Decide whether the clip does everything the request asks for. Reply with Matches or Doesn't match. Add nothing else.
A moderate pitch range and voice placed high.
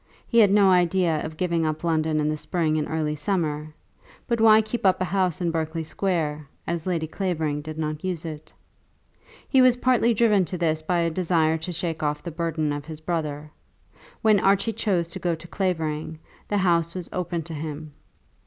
Doesn't match